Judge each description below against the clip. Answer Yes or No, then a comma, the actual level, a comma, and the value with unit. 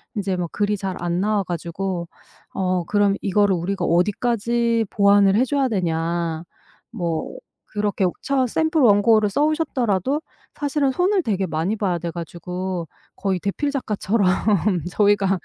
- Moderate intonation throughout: Yes, average, 4.4 semitones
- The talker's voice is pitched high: Yes, high, 200 Hz